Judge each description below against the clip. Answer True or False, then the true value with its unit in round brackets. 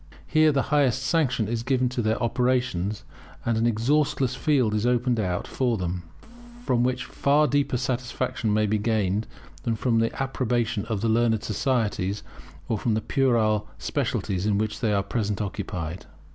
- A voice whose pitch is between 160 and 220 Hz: False (115 Hz)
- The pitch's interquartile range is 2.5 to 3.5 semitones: True (3.1 semitones)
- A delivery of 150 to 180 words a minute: True (170 wpm)